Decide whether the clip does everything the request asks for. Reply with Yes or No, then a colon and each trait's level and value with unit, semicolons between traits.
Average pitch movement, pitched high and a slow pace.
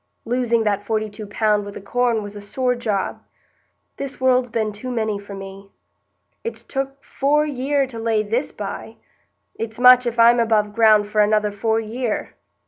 No: average, 3.1 semitones; high, 225 Hz; average, 175 wpm